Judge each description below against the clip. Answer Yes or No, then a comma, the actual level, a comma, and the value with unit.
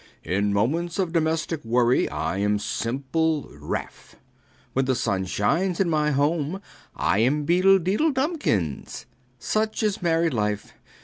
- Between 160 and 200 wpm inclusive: No, slow, 135 wpm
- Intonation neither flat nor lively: No, wide, 7.6 semitones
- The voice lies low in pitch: No, medium, 150 Hz